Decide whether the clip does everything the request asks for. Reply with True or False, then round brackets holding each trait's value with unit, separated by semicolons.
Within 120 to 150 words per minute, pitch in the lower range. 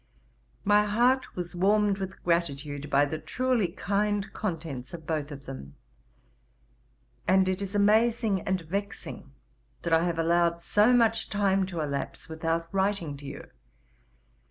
False (140 wpm; 185 Hz)